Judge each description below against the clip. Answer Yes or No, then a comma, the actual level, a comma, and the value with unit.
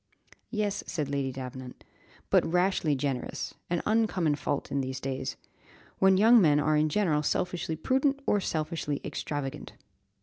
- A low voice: No, medium, 155 Hz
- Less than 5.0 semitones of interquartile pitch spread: No, wide, 5.4 semitones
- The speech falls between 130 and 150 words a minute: Yes, average, 140 wpm